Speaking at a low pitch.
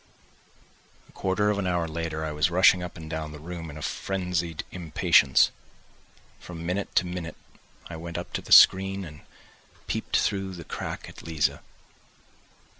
Yes: very low, 85 Hz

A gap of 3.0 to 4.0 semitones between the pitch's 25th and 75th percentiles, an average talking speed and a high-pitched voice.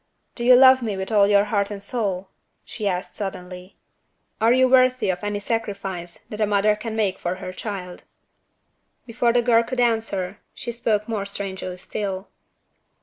Yes: average, 3.3 semitones; average, 170 wpm; high, 205 Hz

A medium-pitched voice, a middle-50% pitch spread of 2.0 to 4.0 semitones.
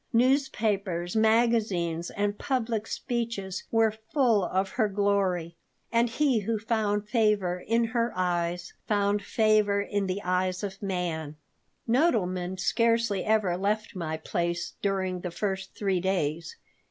No: high, 200 Hz; average, 3.5 semitones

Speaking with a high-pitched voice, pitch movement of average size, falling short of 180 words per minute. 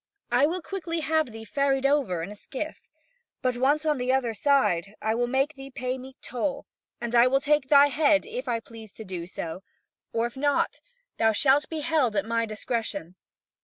No: very high, 255 Hz; average, 4.3 semitones; average, 200 wpm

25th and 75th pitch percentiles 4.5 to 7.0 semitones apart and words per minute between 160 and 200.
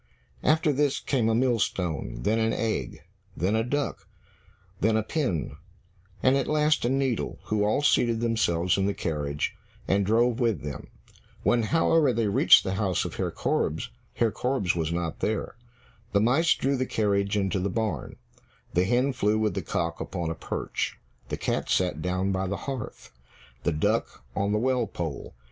Yes: average, 5.1 semitones; average, 175 wpm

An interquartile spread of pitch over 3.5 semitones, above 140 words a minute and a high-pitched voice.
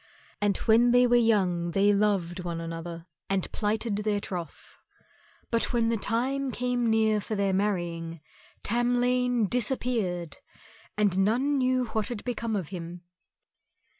No: average, 4.8 semitones; slow, 135 wpm; high, 210 Hz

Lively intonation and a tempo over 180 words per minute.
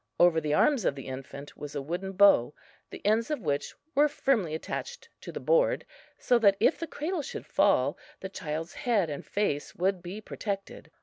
Yes: wide, 8.3 semitones; average, 190 wpm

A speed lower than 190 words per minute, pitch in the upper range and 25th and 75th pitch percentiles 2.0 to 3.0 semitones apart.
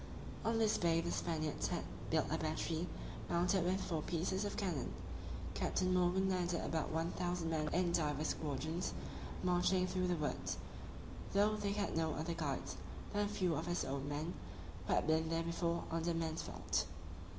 No: average, 170 wpm; medium, 170 Hz; narrow, 2.4 semitones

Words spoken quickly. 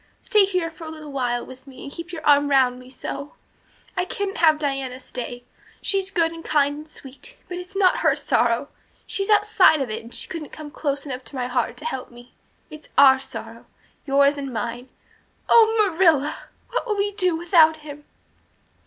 No: average, 195 wpm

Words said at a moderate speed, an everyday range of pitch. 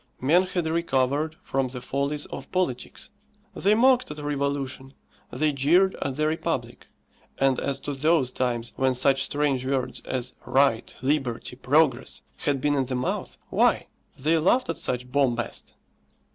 Yes: average, 150 wpm; average, 3.0 semitones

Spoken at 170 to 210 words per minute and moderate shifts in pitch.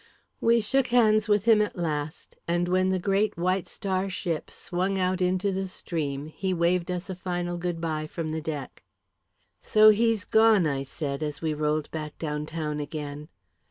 Yes: average, 180 wpm; average, 4.0 semitones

